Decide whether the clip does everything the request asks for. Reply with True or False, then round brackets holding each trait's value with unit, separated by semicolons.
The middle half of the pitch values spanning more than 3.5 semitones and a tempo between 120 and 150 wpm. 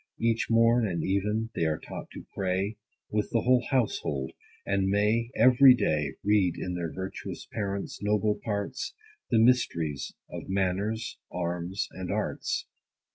True (3.9 semitones; 140 wpm)